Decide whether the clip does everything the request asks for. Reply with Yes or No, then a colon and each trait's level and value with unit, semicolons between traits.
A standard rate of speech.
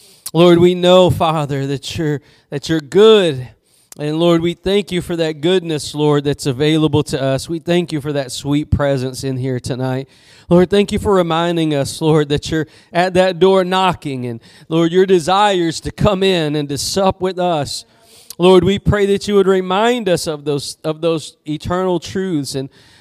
Yes: average, 190 wpm